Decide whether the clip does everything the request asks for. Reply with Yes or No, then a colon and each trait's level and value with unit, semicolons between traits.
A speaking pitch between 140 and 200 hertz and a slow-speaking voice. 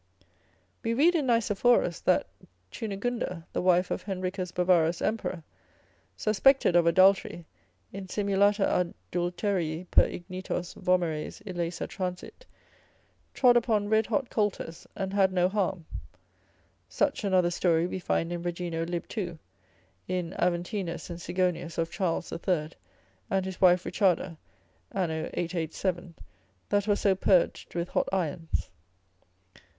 Yes: medium, 185 Hz; slow, 125 wpm